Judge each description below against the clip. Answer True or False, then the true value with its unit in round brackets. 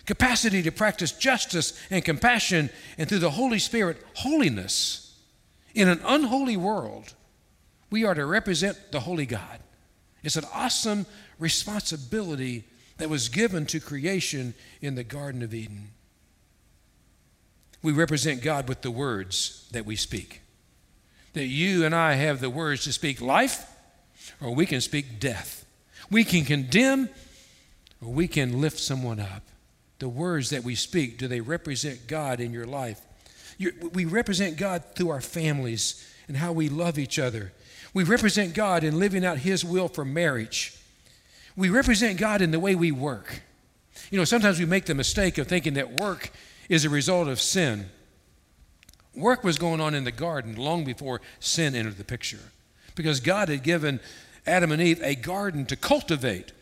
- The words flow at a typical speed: True (160 wpm)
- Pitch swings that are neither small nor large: False (6.4 semitones)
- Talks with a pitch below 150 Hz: False (155 Hz)